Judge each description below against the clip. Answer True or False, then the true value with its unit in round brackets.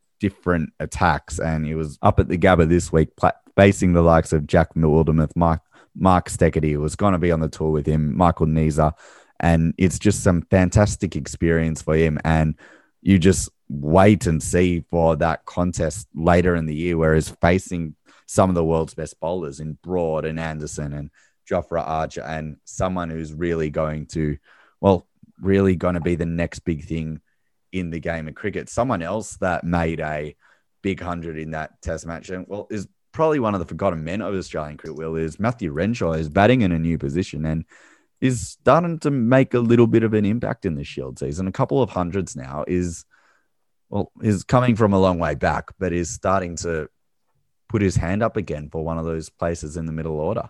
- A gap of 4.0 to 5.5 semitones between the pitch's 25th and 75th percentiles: False (3.3 semitones)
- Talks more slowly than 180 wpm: False (200 wpm)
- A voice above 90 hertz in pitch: False (85 Hz)